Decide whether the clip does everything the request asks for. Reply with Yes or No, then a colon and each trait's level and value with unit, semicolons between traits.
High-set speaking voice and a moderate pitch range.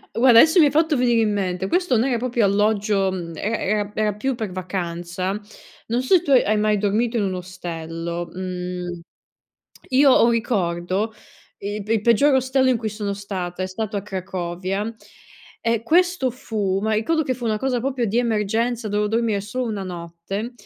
Yes: high, 210 Hz; average, 4.2 semitones